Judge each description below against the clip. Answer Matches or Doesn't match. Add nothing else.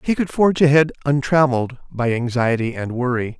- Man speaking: Matches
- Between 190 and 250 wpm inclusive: Doesn't match